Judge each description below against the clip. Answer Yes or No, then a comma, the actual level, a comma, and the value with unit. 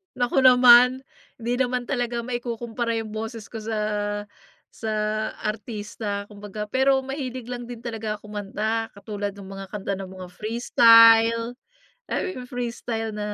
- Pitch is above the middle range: Yes, high, 230 Hz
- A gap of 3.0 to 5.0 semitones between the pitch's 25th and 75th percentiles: No, narrow, 2.6 semitones